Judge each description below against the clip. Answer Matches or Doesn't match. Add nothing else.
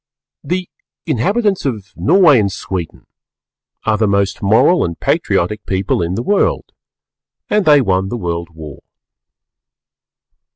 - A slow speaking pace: Matches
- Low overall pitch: Matches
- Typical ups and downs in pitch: Doesn't match